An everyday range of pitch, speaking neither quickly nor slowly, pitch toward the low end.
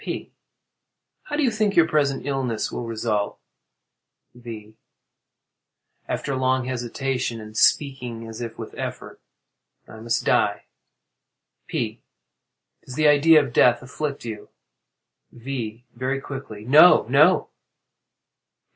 No: average, 3.6 semitones; slow, 115 wpm; low, 125 Hz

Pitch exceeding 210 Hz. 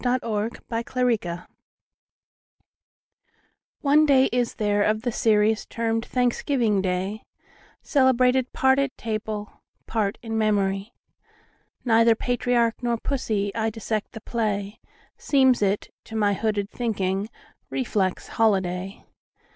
Yes: high, 225 Hz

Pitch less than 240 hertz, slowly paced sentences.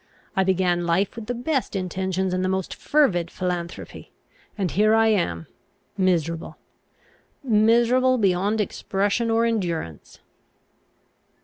Yes: high, 190 Hz; slow, 115 wpm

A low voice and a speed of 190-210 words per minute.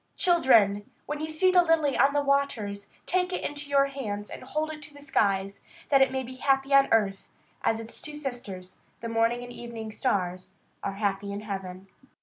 No: high, 245 Hz; average, 195 wpm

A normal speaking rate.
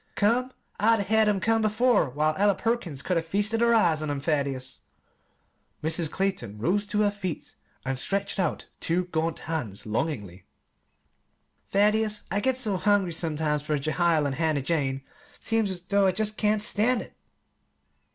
Yes: average, 165 wpm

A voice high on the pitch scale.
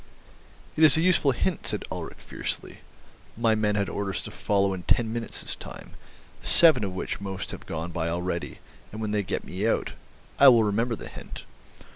No: low, 105 Hz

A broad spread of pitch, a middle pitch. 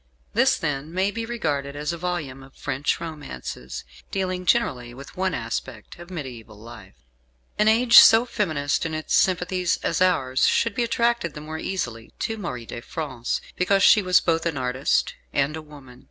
Yes: wide, 6.0 semitones; medium, 155 Hz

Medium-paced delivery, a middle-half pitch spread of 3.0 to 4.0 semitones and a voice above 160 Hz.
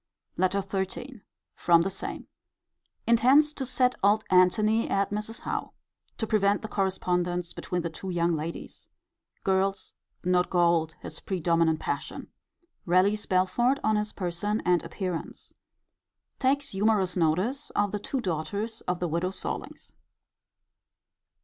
No: slow, 130 wpm; average, 3.5 semitones; high, 190 Hz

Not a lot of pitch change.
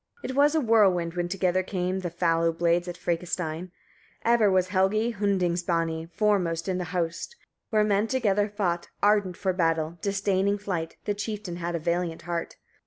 No: average, 3.1 semitones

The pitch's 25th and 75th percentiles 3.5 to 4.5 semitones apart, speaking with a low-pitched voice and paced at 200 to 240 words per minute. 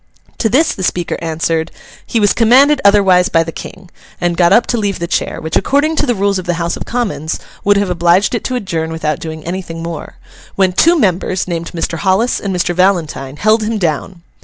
No: average, 4.1 semitones; medium, 185 Hz; fast, 205 wpm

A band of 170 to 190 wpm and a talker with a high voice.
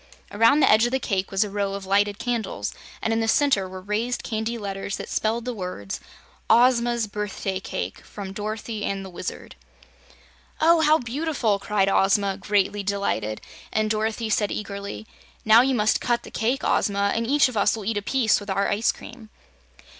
Yes: average, 185 wpm; high, 210 Hz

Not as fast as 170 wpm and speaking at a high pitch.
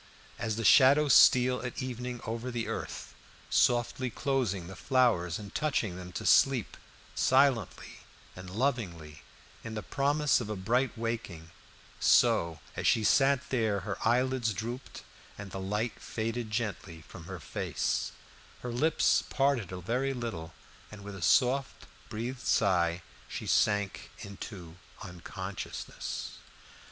No: slow, 135 wpm; low, 115 Hz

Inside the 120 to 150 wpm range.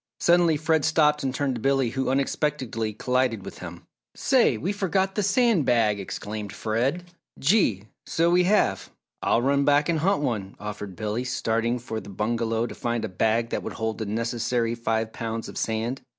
No: average, 180 wpm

